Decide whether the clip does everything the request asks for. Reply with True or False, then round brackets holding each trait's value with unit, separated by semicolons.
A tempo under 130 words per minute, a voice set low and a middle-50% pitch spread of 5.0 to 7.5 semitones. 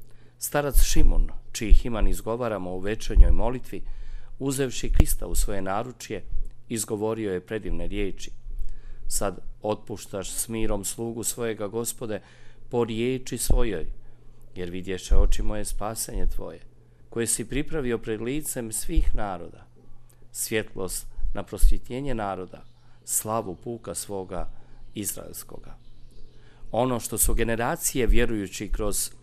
False (110 wpm; 115 Hz; 3.5 semitones)